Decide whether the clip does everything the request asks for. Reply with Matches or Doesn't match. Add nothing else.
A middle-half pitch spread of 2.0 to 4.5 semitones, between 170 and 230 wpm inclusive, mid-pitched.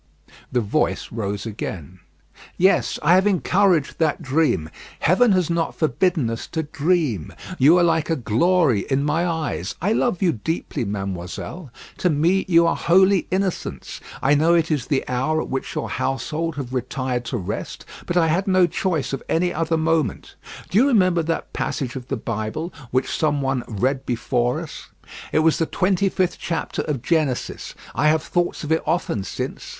Doesn't match